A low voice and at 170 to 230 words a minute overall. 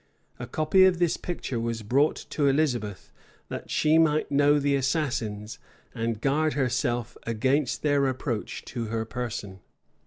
No: low, 130 Hz; average, 145 wpm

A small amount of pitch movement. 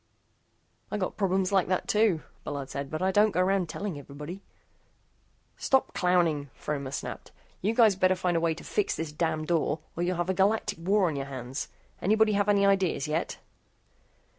No: average, 4.1 semitones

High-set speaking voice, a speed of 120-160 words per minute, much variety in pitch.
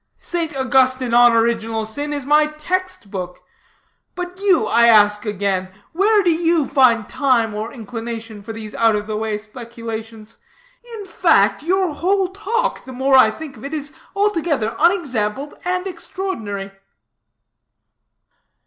Yes: very high, 255 Hz; average, 140 wpm; wide, 7.4 semitones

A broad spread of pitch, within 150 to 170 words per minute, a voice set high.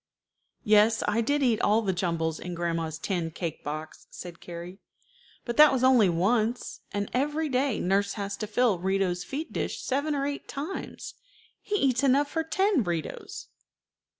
Yes: wide, 7.5 semitones; average, 165 wpm; high, 215 Hz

